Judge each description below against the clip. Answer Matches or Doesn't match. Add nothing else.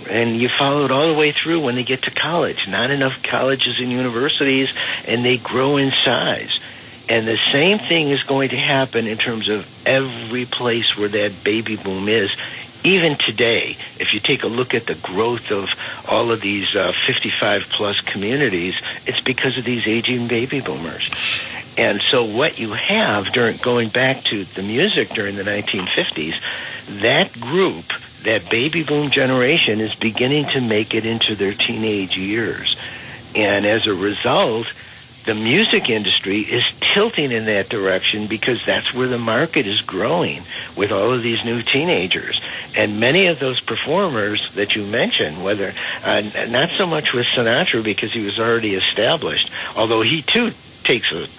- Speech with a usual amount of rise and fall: Matches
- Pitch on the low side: Matches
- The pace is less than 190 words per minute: Matches